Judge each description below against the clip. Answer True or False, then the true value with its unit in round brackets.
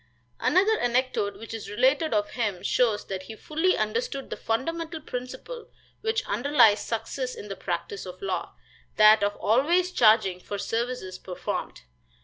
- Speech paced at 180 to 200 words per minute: False (145 wpm)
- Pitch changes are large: True (6.9 semitones)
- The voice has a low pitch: False (235 Hz)